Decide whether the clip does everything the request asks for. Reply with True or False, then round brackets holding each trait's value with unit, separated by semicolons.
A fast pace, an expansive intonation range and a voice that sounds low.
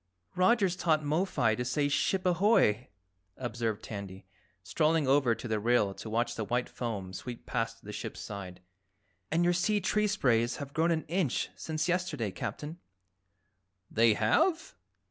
False (155 wpm; 7.5 semitones; 130 Hz)